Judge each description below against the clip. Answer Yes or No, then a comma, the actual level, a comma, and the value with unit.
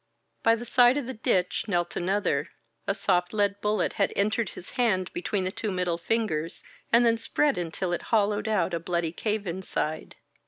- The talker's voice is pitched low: No, high, 200 Hz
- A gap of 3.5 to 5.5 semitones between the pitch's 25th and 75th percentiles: Yes, average, 3.9 semitones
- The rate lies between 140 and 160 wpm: No, average, 185 wpm